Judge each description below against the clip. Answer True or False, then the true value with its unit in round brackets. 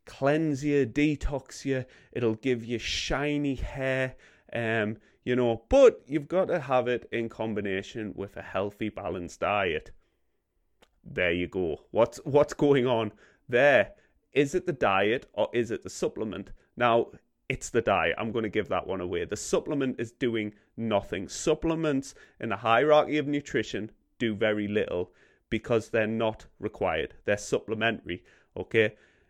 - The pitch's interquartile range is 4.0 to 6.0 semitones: True (4.7 semitones)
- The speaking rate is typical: True (150 wpm)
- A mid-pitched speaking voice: False (120 Hz)